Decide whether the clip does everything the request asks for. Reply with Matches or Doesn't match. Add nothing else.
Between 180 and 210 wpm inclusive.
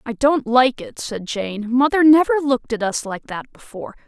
Matches